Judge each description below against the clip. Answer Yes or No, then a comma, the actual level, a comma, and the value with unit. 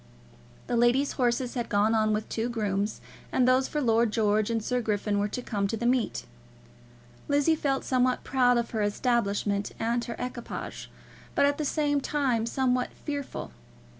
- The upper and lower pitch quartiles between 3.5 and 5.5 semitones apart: No, average, 3.1 semitones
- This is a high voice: Yes, high, 240 Hz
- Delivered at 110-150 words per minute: No, average, 170 wpm